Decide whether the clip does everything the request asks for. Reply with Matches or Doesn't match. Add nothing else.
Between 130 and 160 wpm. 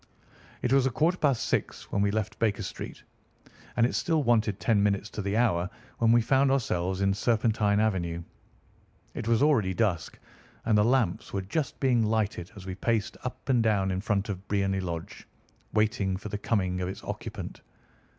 Doesn't match